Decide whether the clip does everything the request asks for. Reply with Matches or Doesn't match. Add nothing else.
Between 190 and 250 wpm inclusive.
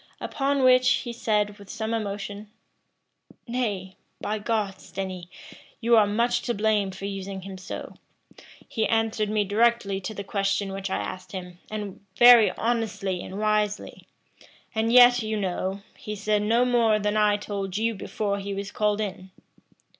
Doesn't match